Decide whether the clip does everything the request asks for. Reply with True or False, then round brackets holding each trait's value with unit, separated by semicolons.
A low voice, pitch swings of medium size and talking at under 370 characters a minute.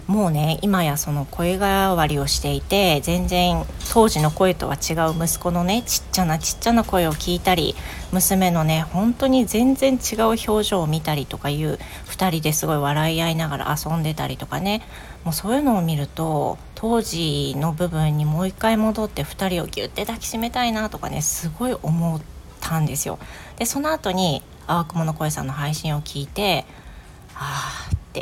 False (170 Hz; 4.9 semitones; 335 characters per minute)